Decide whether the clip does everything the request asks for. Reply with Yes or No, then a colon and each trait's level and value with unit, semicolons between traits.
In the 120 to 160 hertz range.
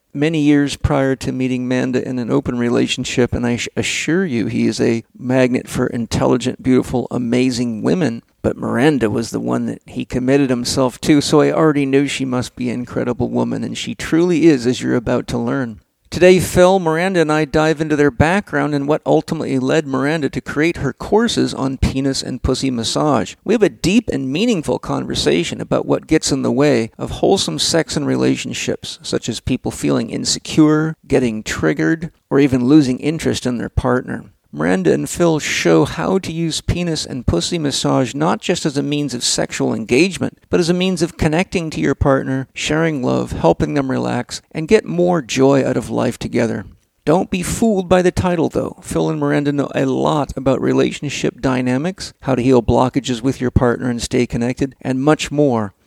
Yes: low, 135 Hz